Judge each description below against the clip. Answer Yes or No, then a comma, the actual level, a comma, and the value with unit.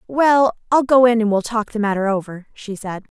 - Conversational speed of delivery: No, fast, 225 wpm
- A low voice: No, high, 225 Hz